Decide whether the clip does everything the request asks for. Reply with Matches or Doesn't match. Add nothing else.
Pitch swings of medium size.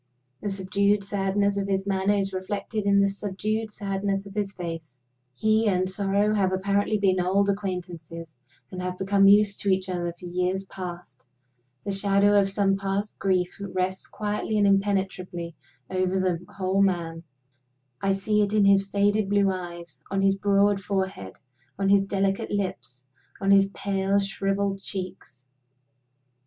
Doesn't match